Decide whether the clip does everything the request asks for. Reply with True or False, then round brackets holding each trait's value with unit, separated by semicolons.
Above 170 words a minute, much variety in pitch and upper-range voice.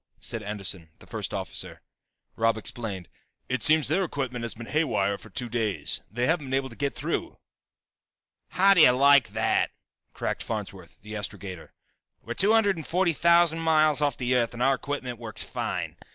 False (180 wpm; 5.8 semitones; 125 Hz)